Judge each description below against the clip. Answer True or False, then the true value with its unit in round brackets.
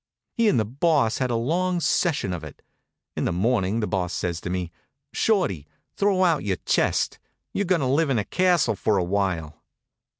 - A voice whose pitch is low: True (115 Hz)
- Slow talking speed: False (195 wpm)